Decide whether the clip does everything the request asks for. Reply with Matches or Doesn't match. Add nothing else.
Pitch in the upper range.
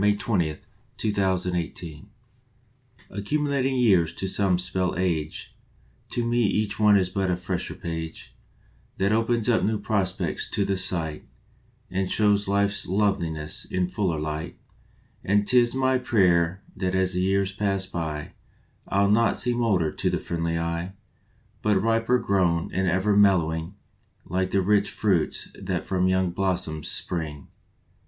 Doesn't match